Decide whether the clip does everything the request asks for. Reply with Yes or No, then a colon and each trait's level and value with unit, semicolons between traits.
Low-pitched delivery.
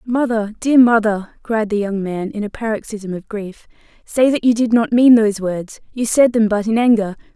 No: high, 220 Hz